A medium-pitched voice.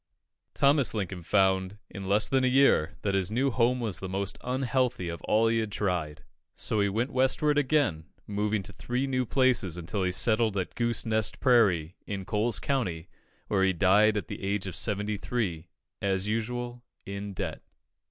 No: low, 105 Hz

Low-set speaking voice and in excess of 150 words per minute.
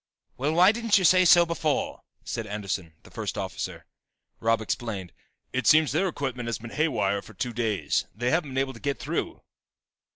Yes: low, 130 Hz; average, 185 wpm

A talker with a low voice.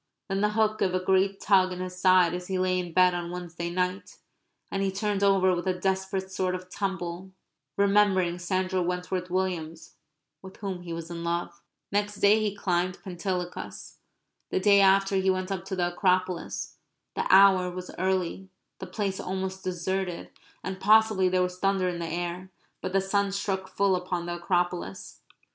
No: medium, 185 Hz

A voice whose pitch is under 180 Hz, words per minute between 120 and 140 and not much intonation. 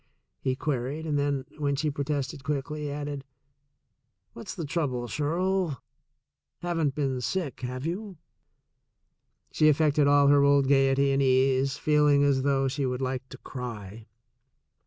Yes: medium, 140 Hz; slow, 135 wpm; narrow, 2.2 semitones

